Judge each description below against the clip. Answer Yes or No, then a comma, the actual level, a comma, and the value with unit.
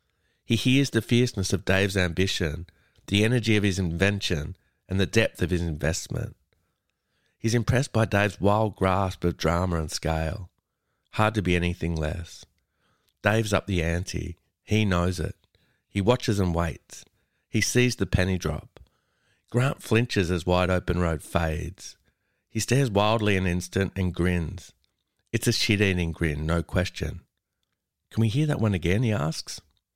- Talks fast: No, average, 155 wpm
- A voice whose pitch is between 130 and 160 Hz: No, very low, 95 Hz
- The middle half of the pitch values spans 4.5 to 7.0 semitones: No, average, 3.9 semitones